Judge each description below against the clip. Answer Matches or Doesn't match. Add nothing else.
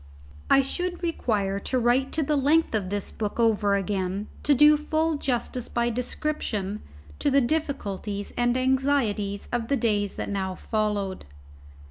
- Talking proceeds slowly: Doesn't match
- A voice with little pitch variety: Doesn't match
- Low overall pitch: Doesn't match